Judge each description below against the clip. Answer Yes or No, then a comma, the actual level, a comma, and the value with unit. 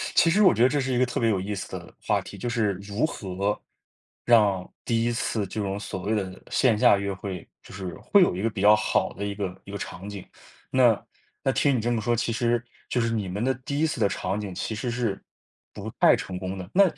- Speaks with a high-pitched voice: No, low, 105 Hz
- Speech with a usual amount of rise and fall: Yes, average, 3.6 semitones